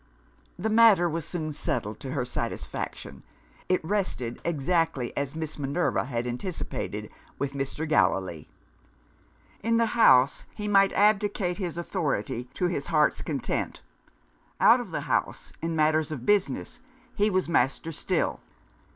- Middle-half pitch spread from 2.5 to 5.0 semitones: No, wide, 5.6 semitones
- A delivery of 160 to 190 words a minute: No, slow, 135 wpm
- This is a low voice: No, medium, 160 Hz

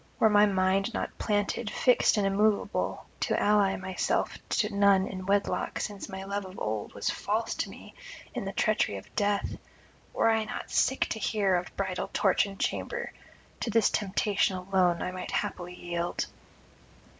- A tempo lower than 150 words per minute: No, average, 170 wpm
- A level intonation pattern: Yes, narrow, 1.8 semitones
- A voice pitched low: No, high, 195 Hz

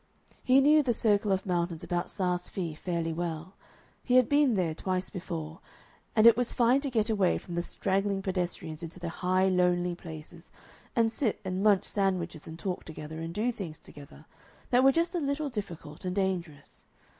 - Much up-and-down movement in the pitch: No, average, 4.6 semitones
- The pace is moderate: Yes, average, 185 wpm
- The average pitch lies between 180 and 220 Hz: Yes, medium, 185 Hz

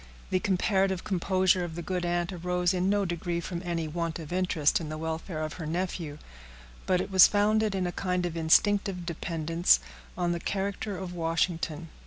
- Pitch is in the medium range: Yes, medium, 175 Hz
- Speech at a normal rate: Yes, average, 185 wpm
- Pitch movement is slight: Yes, narrow, 2.1 semitones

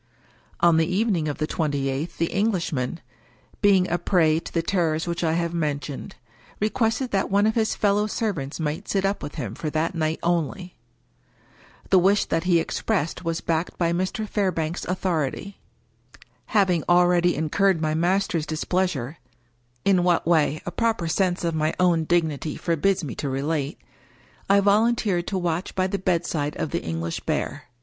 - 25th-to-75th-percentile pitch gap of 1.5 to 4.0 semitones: Yes, average, 3.5 semitones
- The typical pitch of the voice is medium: Yes, medium, 170 Hz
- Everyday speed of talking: Yes, average, 175 wpm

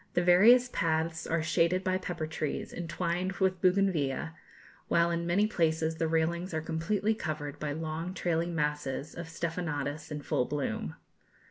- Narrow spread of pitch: Yes, narrow, 2.2 semitones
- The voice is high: No, medium, 165 Hz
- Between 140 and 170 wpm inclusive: Yes, average, 150 wpm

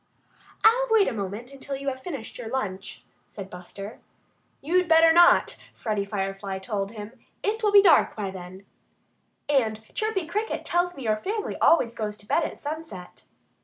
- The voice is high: Yes, high, 240 Hz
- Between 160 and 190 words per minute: Yes, average, 170 wpm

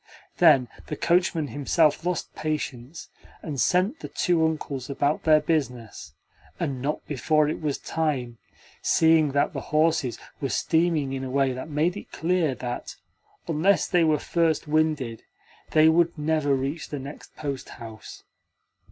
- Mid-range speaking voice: Yes, medium, 150 Hz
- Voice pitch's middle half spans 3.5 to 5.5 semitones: No, average, 3.0 semitones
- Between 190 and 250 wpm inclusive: No, average, 145 wpm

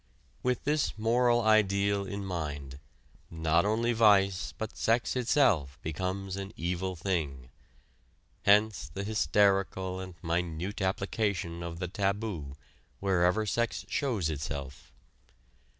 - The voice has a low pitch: Yes, very low, 95 Hz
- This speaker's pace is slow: Yes, slow, 110 wpm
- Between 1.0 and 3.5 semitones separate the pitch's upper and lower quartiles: No, average, 4.2 semitones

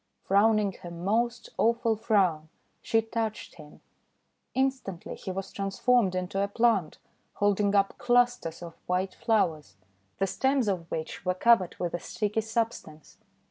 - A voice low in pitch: No, high, 200 Hz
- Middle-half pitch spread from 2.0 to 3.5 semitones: No, average, 4.0 semitones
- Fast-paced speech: No, average, 140 wpm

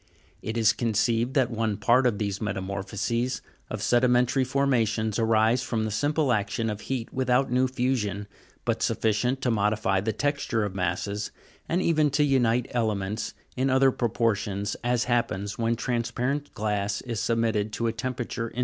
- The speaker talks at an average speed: Yes, average, 165 wpm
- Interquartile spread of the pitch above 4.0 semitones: No, average, 3.2 semitones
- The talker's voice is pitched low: Yes, low, 115 Hz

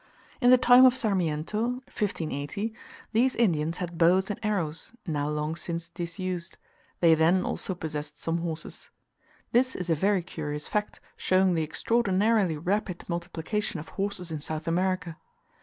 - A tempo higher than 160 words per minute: No, average, 145 wpm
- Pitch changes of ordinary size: Yes, average, 4.2 semitones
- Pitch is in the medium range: Yes, medium, 175 Hz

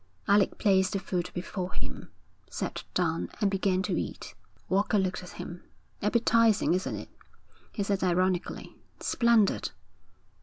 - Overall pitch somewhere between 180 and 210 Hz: Yes, high, 190 Hz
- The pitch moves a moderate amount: No, narrow, 2.0 semitones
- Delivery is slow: Yes, slow, 130 wpm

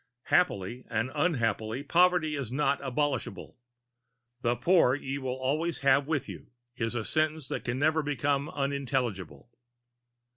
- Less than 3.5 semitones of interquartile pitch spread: No, average, 3.8 semitones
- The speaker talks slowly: Yes, slow, 125 wpm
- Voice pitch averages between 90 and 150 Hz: Yes, medium, 140 Hz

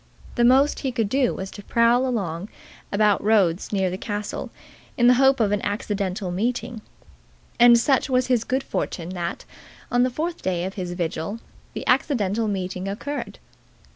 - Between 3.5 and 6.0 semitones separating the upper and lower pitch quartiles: Yes, average, 4.7 semitones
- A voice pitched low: No, high, 215 Hz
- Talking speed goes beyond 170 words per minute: No, average, 165 wpm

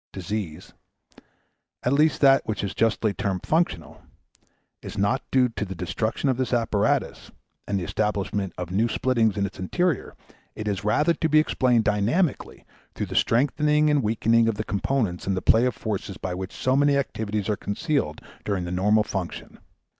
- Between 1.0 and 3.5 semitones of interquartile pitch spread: No, average, 4.9 semitones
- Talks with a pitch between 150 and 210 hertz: No, low, 110 Hz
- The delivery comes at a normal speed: Yes, average, 175 wpm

